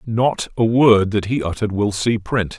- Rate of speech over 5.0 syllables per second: No, 4.6 syllables/s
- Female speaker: No, male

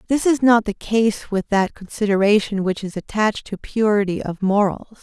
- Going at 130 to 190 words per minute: Yes, average, 180 wpm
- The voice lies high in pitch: Yes, high, 205 Hz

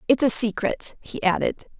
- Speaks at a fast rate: No, average, 165 wpm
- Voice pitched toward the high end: Yes, high, 235 Hz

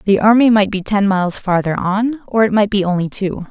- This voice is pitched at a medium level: No, high, 200 Hz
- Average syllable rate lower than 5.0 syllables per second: No, 5.5 syllables/s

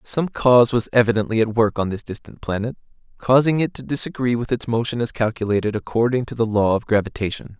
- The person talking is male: Yes, male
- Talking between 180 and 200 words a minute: Yes, average, 195 wpm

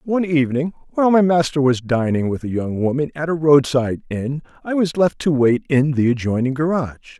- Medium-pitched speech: Yes, medium, 145 Hz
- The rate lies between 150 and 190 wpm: No, average, 200 wpm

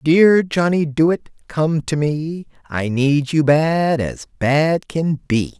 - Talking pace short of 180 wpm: Yes, average, 150 wpm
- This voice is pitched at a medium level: Yes, medium, 155 Hz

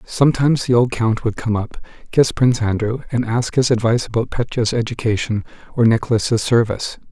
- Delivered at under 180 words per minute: Yes, average, 170 wpm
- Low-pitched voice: Yes, low, 115 Hz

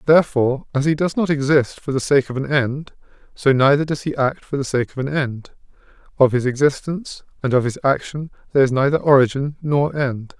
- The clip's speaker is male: Yes, male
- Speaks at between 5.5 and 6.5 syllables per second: Yes, 5.6 syllables/s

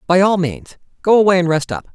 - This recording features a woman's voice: No, male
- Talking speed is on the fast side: Yes, fast, 245 wpm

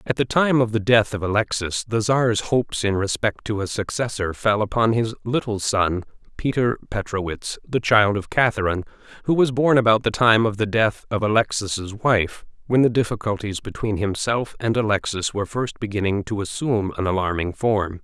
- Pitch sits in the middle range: No, low, 110 Hz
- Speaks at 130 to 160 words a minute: No, average, 180 wpm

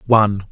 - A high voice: No, low, 105 Hz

